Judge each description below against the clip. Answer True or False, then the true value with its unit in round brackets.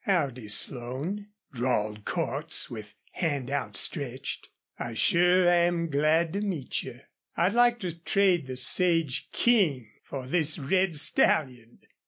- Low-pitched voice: False (155 Hz)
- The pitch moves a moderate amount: False (5.7 semitones)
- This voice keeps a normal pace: False (125 wpm)